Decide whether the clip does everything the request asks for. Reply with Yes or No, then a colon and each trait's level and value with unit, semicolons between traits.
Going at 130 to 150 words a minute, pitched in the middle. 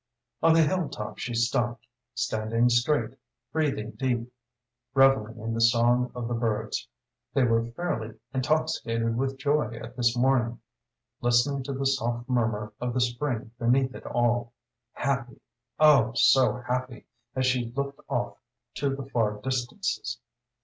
No: average, 140 wpm; low, 120 Hz